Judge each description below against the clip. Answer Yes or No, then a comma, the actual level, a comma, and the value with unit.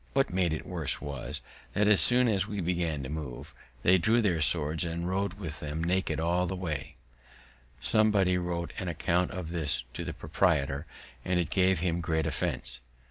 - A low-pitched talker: Yes, very low, 85 Hz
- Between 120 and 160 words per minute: No, average, 185 wpm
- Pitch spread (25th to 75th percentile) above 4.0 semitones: No, average, 3.1 semitones